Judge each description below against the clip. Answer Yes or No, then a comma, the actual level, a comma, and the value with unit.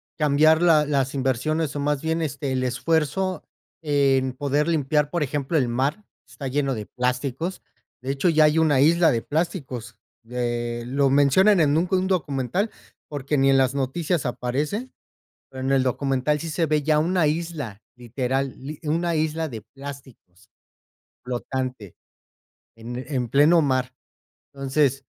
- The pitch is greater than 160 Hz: No, medium, 140 Hz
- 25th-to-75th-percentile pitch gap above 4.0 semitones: No, average, 3.4 semitones